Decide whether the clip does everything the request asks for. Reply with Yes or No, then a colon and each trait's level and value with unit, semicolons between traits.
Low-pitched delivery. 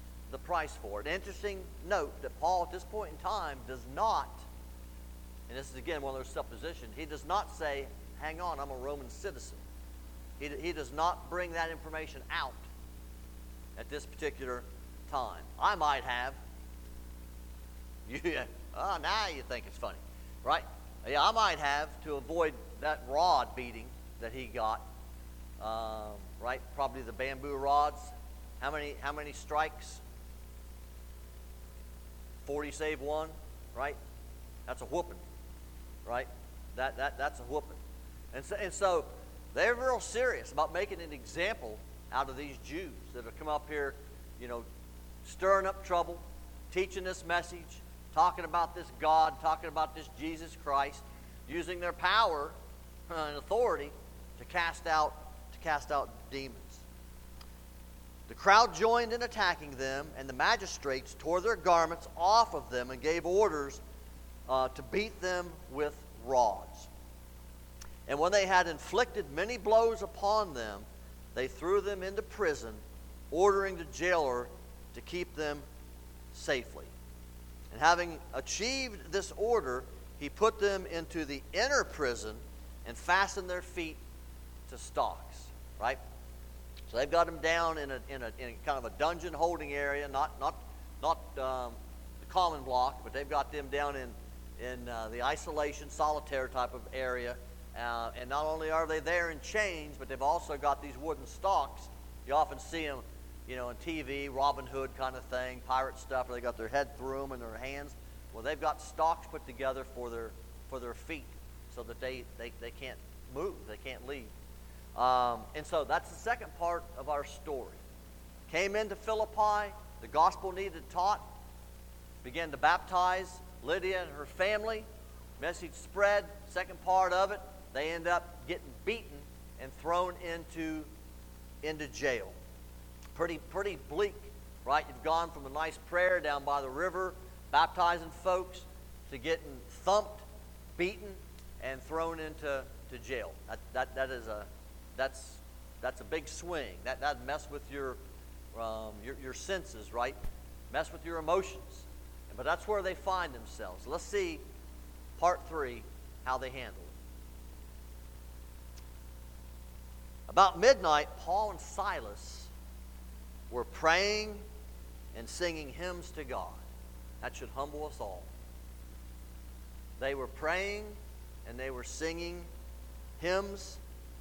Yes: low, 120 Hz